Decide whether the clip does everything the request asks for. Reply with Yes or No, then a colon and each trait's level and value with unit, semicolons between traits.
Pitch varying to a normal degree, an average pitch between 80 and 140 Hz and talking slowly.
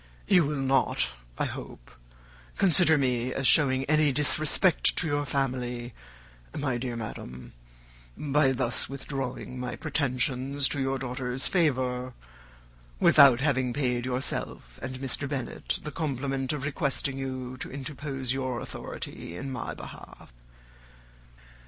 No: narrow, 2.2 semitones; low, 135 Hz; slow, 125 wpm